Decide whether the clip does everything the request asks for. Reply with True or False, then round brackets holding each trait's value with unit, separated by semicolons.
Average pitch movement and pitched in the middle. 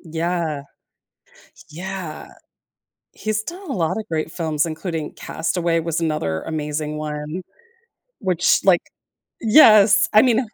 True (4.3 semitones; 165 Hz)